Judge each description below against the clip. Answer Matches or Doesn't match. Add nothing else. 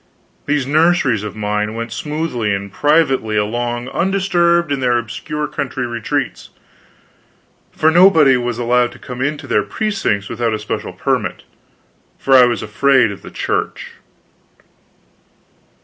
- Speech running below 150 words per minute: Matches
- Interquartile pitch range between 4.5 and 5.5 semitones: Matches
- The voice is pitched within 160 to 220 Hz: Doesn't match